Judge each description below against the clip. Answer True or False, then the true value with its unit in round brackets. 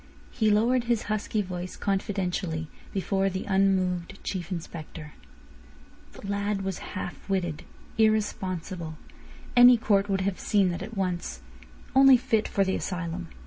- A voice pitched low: False (195 Hz)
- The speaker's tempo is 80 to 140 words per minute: True (135 wpm)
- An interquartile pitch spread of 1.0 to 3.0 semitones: True (2.7 semitones)